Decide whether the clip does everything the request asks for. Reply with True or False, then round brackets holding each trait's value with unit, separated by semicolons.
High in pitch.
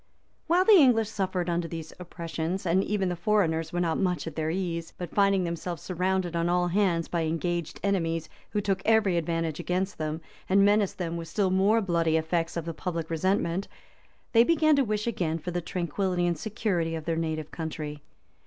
False (175 Hz)